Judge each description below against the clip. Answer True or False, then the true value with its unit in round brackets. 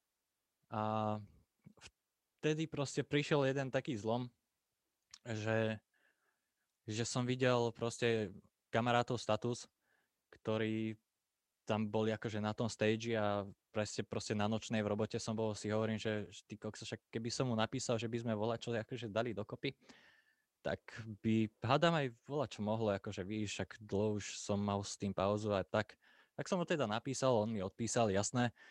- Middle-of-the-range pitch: False (110 Hz)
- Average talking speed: True (155 wpm)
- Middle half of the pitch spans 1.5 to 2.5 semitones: True (2.1 semitones)